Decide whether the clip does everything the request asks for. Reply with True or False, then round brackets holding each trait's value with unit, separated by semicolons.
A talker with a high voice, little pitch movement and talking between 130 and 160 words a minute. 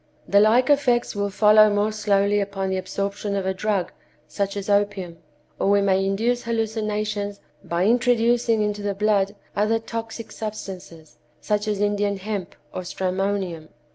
True (205 Hz; 1.7 semitones; 150 wpm)